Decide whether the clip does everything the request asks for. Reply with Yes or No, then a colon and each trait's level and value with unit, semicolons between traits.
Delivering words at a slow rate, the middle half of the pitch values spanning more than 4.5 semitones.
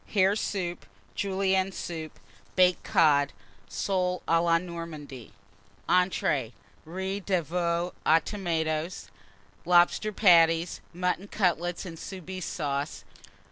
No: slow, 100 wpm; narrow, 2.4 semitones